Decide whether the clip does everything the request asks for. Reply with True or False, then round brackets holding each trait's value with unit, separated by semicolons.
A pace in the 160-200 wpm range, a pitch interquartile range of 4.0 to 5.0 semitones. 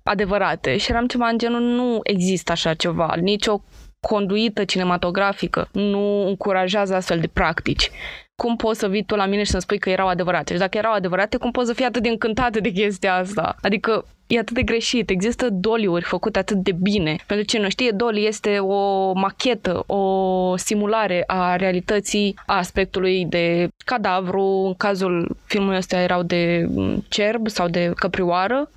False (170 wpm; 3.0 semitones)